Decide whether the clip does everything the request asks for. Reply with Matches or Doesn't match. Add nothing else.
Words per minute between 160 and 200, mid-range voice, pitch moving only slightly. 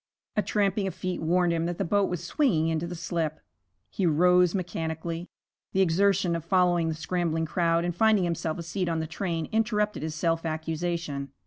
Matches